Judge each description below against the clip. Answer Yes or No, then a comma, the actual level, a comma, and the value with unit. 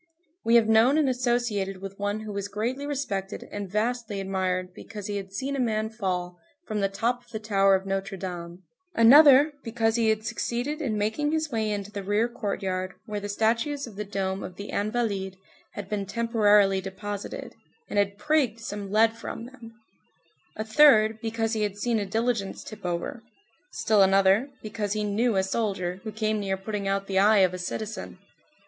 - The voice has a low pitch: No, high, 210 Hz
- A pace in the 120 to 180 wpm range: No, average, 190 wpm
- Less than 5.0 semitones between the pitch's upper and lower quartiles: Yes, average, 2.7 semitones